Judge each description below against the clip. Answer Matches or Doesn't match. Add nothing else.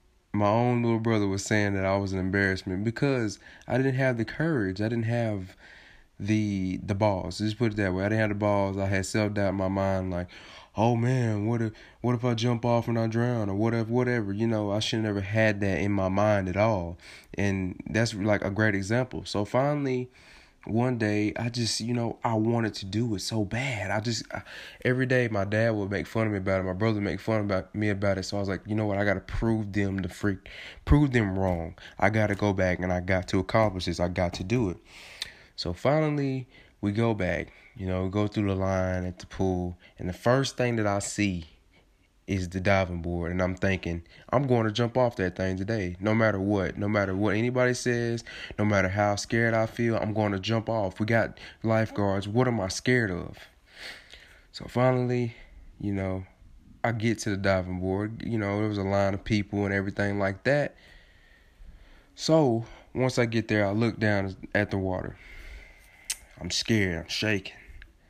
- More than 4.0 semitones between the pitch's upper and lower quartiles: Doesn't match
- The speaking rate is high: Matches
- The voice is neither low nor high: Doesn't match